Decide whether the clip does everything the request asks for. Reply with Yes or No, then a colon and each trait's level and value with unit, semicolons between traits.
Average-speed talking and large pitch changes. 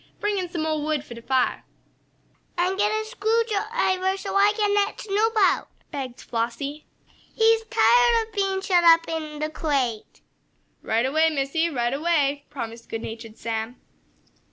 Yes: average, 160 wpm; wide, 7.0 semitones